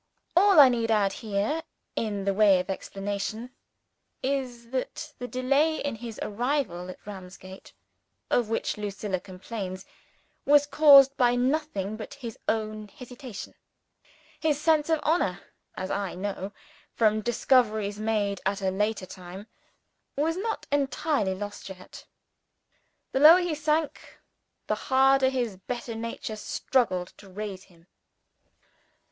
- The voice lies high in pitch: Yes, high, 225 Hz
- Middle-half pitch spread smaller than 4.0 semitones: No, wide, 5.6 semitones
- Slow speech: Yes, slow, 130 wpm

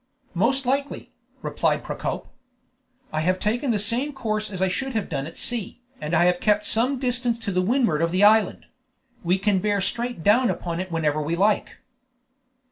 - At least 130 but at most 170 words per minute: No, average, 180 wpm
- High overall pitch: Yes, high, 205 Hz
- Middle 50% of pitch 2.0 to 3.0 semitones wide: No, average, 5.2 semitones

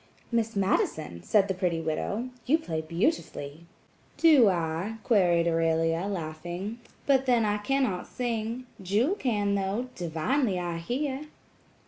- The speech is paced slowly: Yes, slow, 120 wpm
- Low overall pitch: No, high, 200 Hz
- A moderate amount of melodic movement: No, wide, 6.4 semitones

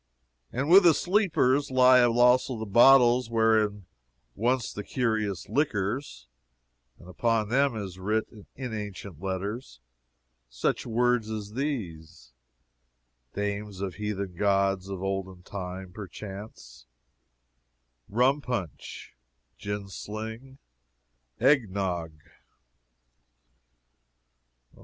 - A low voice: Yes, low, 105 Hz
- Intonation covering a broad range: No, average, 4.3 semitones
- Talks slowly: Yes, slow, 90 wpm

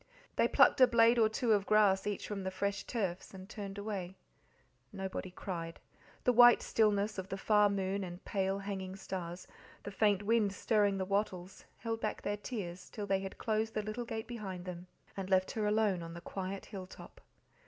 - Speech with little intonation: Yes, narrow, 2.2 semitones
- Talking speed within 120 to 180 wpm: No, average, 195 wpm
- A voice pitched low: No, high, 200 Hz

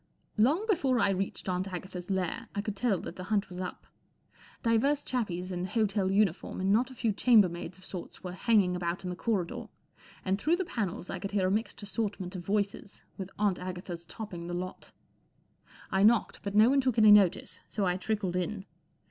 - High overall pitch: Yes, high, 195 Hz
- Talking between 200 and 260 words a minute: Yes, fast, 205 wpm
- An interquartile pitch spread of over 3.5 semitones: No, average, 3.2 semitones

